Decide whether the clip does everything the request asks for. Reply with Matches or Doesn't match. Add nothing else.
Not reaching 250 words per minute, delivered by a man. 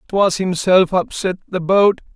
Matches